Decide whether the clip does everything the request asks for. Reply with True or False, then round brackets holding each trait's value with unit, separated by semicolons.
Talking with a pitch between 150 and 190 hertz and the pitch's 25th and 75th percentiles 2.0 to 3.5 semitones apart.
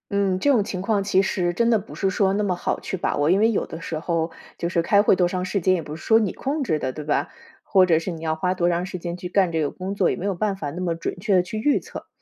True (185 Hz; 2.9 semitones)